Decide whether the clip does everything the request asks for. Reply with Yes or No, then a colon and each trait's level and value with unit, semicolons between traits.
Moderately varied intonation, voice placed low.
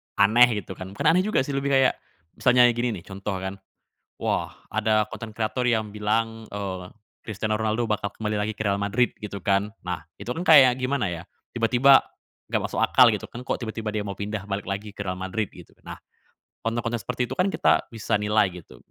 Yes: average, 3.1 semitones; low, 110 Hz